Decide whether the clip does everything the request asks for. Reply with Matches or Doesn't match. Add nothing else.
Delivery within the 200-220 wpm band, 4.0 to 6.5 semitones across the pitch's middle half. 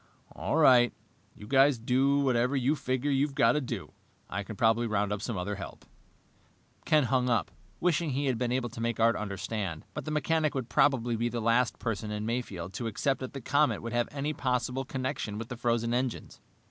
Doesn't match